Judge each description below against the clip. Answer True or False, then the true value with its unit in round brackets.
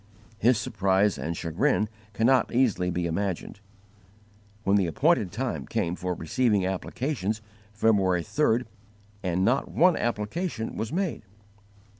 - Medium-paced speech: False (120 wpm)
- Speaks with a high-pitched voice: False (105 Hz)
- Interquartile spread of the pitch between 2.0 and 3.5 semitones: False (5.5 semitones)